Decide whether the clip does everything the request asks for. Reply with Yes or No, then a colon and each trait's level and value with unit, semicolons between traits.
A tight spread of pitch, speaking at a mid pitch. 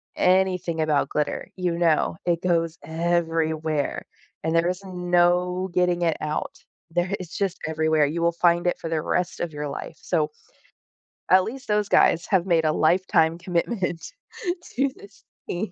Yes: narrow, 2.1 semitones; medium, 170 Hz